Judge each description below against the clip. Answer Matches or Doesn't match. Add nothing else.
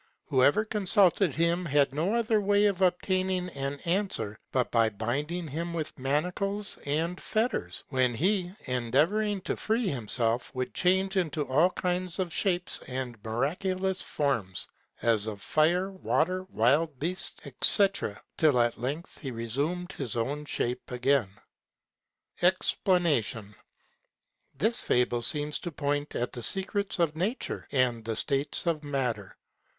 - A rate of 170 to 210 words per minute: Doesn't match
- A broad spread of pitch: Matches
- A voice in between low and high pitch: Matches